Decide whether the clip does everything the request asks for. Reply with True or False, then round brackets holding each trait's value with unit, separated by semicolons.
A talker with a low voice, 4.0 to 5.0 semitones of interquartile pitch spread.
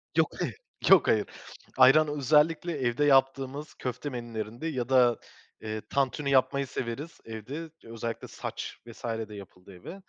True (130 Hz; 4.3 semitones)